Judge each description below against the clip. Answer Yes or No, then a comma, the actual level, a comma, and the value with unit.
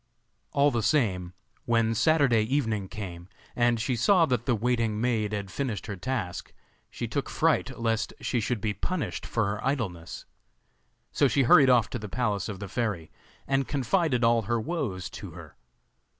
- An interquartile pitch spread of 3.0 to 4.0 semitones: Yes, average, 3.7 semitones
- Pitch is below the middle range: Yes, low, 115 Hz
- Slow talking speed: No, average, 170 wpm